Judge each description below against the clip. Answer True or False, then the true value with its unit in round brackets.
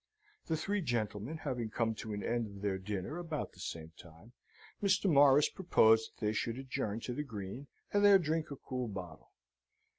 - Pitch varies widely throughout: True (6.5 semitones)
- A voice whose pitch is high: False (120 Hz)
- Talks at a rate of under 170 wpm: False (185 wpm)